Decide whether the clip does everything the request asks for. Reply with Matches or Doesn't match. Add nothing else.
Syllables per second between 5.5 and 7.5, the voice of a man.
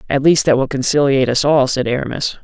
Matches